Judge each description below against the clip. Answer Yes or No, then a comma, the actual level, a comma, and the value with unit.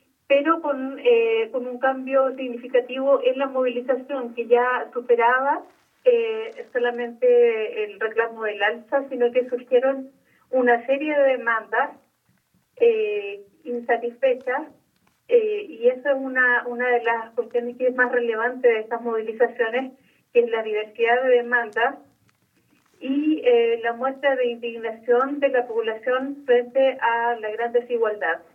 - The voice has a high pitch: Yes, very high, 250 Hz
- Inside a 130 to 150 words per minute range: Yes, average, 135 wpm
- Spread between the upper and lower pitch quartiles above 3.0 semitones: No, narrow, 2.6 semitones